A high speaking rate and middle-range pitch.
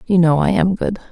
Yes: fast, 270 wpm; medium, 180 Hz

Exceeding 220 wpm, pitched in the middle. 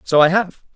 Yes: fast, 240 wpm; medium, 175 Hz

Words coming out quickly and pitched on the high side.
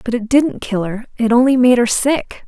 Yes: fast, 240 wpm; high, 240 Hz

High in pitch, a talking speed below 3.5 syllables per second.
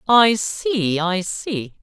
Yes: high, 205 Hz; 2.4 syllables/s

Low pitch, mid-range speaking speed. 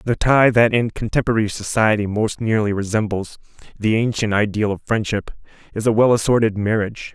Yes: low, 110 Hz; average, 160 wpm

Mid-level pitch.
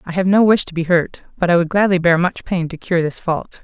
Yes: medium, 175 Hz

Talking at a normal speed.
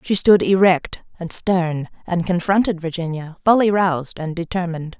Yes: average, 145 wpm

